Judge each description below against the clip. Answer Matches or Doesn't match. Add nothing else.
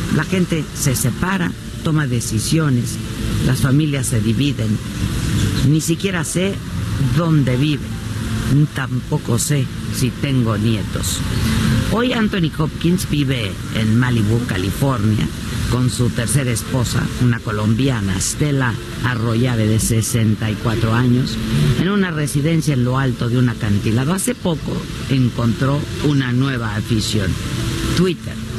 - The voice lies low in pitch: Matches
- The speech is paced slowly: Matches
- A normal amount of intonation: Matches